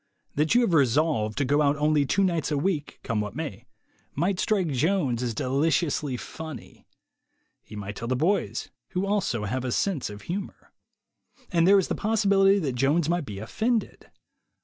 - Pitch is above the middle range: No, medium, 150 Hz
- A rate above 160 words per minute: Yes, average, 175 wpm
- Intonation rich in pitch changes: Yes, wide, 6.7 semitones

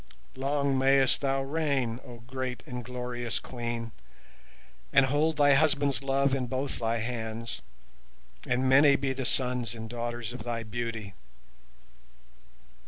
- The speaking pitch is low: Yes, low, 125 Hz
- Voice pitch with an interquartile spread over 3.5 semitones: No, narrow, 2.6 semitones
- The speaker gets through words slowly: Yes, slow, 130 wpm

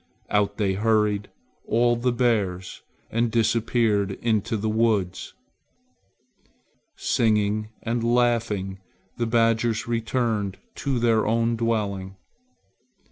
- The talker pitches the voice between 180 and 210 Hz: No, low, 110 Hz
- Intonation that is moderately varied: No, narrow, 2.3 semitones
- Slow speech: Yes, slow, 95 wpm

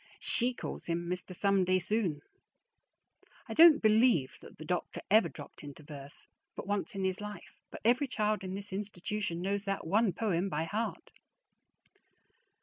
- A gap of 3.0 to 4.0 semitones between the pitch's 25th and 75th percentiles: Yes, average, 3.6 semitones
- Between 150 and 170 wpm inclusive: Yes, average, 155 wpm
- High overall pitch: Yes, high, 195 Hz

